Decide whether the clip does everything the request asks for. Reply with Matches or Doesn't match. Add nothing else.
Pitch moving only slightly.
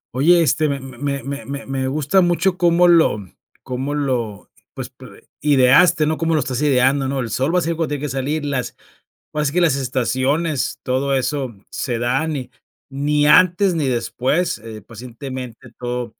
Doesn't match